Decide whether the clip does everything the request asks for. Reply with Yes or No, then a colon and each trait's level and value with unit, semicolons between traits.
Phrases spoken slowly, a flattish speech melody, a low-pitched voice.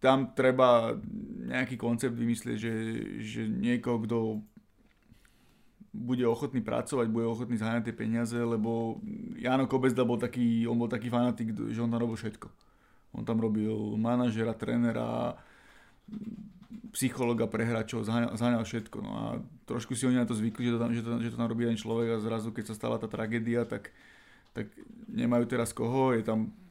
No: fast, 165 wpm; narrow, 1.8 semitones; low, 115 Hz